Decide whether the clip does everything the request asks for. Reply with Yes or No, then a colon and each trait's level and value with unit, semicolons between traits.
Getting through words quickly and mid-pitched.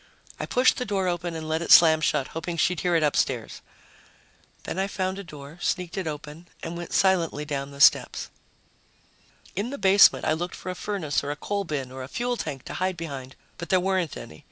Yes: fast, 215 wpm; medium, 170 Hz